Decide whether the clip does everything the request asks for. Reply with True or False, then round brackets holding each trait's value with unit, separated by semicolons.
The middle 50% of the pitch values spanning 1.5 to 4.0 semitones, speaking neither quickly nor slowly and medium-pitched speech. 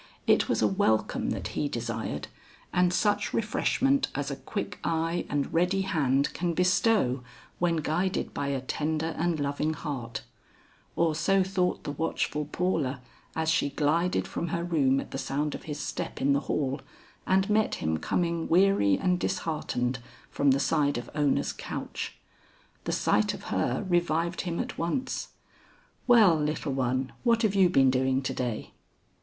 False (4.7 semitones; 160 wpm; 160 Hz)